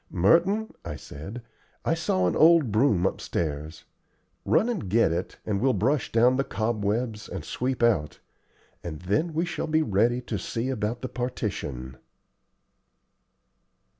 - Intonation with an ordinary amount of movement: No, wide, 6.2 semitones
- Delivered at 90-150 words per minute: Yes, average, 140 wpm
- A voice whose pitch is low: Yes, low, 115 Hz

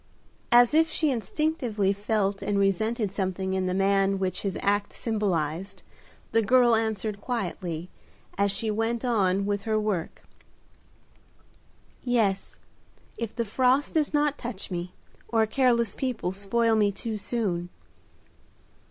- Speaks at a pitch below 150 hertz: No, high, 210 Hz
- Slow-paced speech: Yes, slow, 130 wpm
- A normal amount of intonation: Yes, average, 3.4 semitones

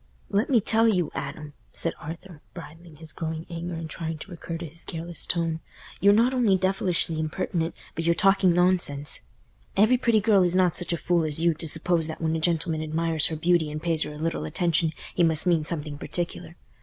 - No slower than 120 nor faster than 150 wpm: No, fast, 205 wpm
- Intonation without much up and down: Yes, narrow, 2.2 semitones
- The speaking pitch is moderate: Yes, medium, 165 Hz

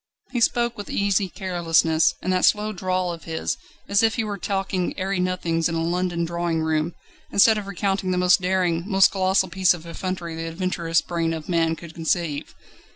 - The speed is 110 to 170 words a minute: No, average, 190 wpm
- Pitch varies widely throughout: No, narrow, 2.6 semitones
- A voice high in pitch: No, medium, 180 Hz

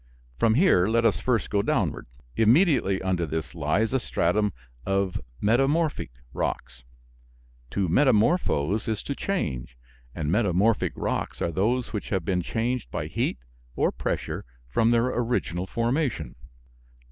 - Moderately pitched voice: No, low, 105 Hz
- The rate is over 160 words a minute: No, slow, 135 wpm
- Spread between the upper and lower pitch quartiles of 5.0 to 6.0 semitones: Yes, wide, 5.4 semitones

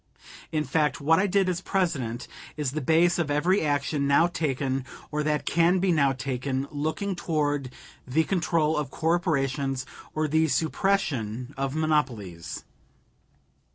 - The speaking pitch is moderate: Yes, medium, 150 Hz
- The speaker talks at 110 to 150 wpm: Yes, average, 140 wpm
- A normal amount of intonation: Yes, average, 3.4 semitones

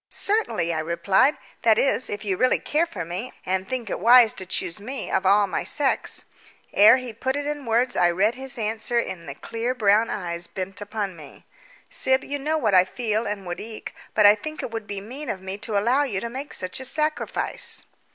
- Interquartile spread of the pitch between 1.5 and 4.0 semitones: No, average, 5.2 semitones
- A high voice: Yes, high, 220 Hz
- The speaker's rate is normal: No, fast, 220 wpm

